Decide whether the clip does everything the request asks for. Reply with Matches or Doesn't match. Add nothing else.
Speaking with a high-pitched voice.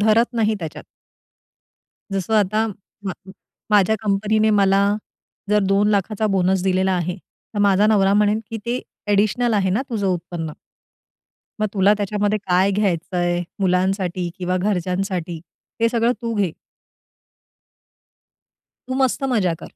Matches